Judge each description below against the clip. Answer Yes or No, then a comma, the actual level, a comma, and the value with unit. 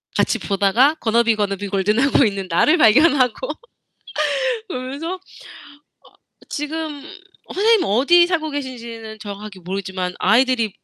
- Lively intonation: Yes, wide, 6.5 semitones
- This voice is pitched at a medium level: No, high, 235 Hz